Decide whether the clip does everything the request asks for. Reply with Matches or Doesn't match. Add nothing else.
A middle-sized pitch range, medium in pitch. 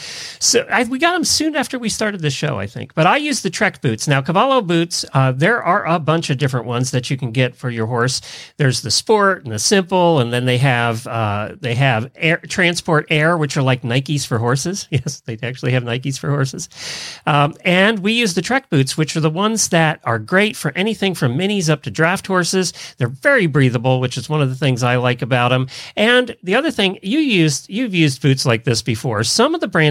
Doesn't match